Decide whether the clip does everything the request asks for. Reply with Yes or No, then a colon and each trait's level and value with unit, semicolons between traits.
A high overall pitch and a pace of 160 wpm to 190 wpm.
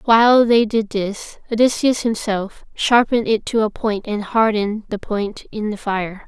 Yes: high, 220 Hz; average, 170 wpm